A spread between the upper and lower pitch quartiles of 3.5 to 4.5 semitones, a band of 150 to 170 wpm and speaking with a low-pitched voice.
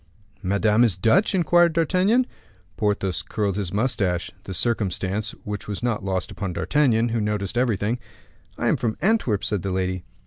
Yes: average, 4.0 semitones; average, 160 wpm; low, 105 Hz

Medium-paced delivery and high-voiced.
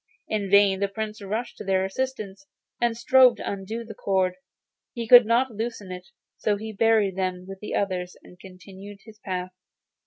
Yes: average, 180 wpm; high, 200 Hz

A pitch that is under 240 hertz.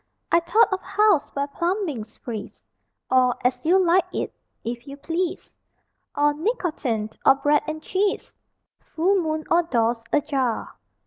No: very high, 310 Hz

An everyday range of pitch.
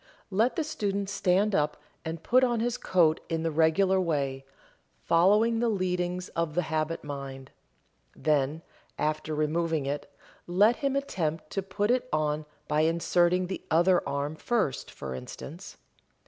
Yes: average, 4.4 semitones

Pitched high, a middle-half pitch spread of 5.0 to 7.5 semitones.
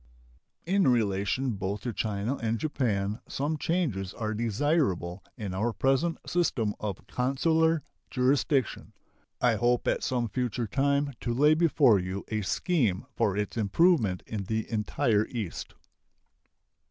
No: low, 120 Hz; wide, 5.4 semitones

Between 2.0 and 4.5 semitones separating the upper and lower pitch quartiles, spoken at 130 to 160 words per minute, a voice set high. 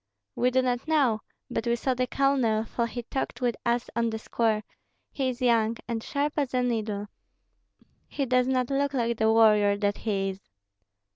No: narrow, 2.5 semitones; average, 190 wpm; high, 235 Hz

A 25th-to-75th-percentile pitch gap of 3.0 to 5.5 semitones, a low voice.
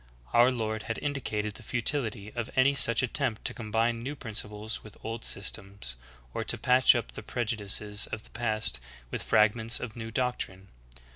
No: narrow, 2.4 semitones; low, 115 Hz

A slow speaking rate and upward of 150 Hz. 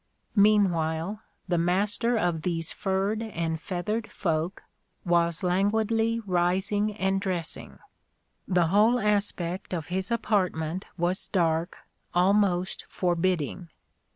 Yes: slow, 100 wpm; medium, 185 Hz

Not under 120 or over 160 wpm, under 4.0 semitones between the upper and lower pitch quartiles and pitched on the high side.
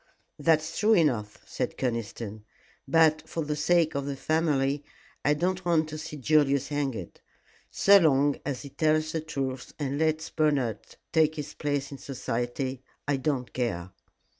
No: average, 155 wpm; average, 2.9 semitones; medium, 145 Hz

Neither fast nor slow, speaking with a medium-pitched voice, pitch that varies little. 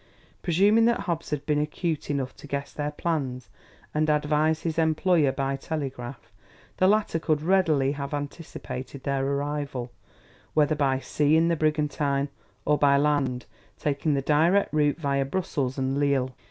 Yes: average, 155 wpm; medium, 150 Hz; narrow, 2.3 semitones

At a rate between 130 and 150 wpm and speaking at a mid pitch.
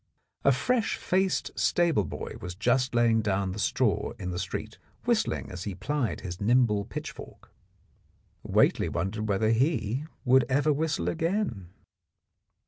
No: slow, 135 wpm; low, 115 Hz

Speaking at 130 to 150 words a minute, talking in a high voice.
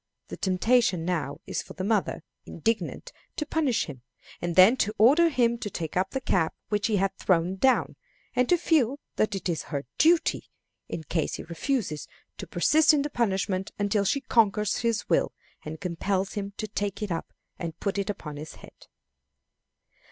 No: average, 180 wpm; high, 200 Hz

